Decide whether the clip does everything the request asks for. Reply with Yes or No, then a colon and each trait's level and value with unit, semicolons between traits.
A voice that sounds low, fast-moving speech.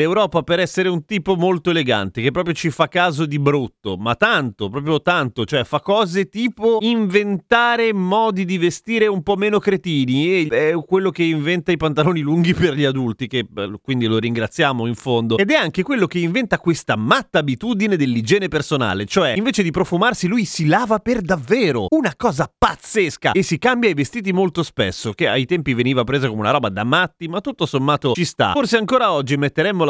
No: medium, 170 Hz; fast, 195 wpm